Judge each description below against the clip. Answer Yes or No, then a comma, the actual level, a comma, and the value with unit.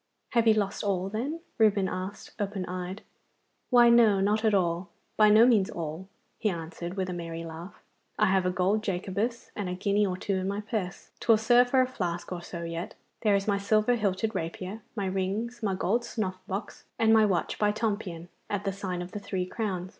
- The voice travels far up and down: No, average, 3.0 semitones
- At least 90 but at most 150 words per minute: No, fast, 205 wpm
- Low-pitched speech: No, high, 195 Hz